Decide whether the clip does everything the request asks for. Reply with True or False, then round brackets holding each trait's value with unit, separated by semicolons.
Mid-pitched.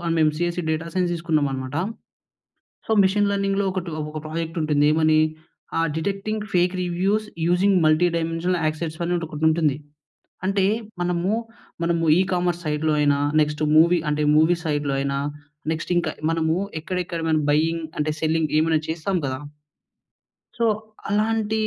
True (165 Hz)